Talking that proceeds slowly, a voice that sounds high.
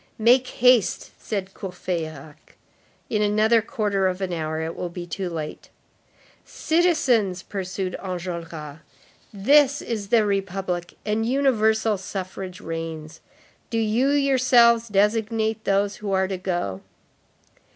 Yes: slow, 120 wpm; high, 200 Hz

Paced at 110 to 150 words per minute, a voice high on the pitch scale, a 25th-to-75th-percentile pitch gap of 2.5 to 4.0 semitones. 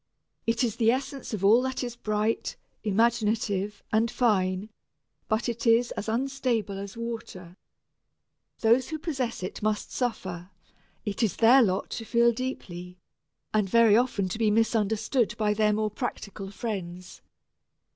Yes: average, 145 wpm; high, 220 Hz; average, 2.8 semitones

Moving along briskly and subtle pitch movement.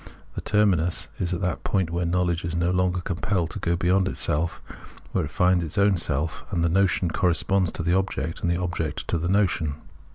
Yes: fast, 215 wpm; narrow, 1.8 semitones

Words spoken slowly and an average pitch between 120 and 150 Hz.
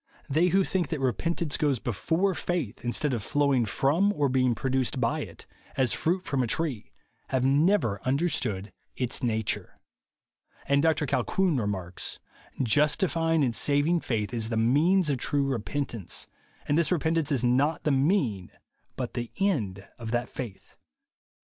No: average, 155 wpm; low, 135 Hz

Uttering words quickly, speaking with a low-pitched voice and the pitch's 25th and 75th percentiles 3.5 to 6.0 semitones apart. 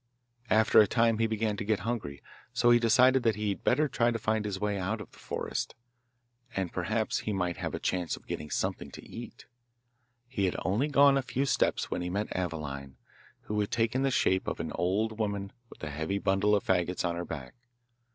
Yes: fast, 215 wpm; low, 105 Hz; average, 4.1 semitones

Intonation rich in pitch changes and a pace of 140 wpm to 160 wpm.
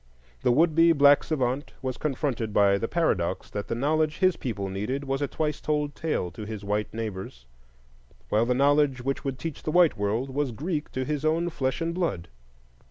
No: wide, 5.7 semitones; average, 195 wpm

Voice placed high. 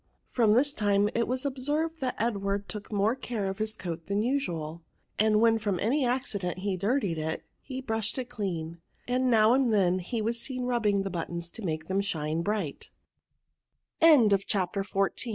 Yes: high, 215 Hz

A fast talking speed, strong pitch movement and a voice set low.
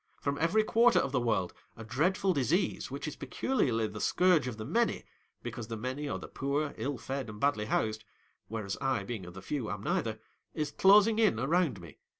Yes: fast, 210 wpm; wide, 6.7 semitones; low, 130 Hz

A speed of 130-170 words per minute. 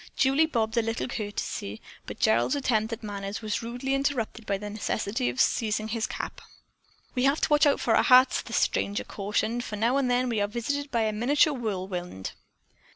No: average, 195 wpm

